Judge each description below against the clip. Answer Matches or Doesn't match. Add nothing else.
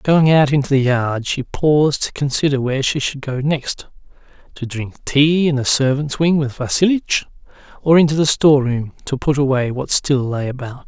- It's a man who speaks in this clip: Matches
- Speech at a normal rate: Matches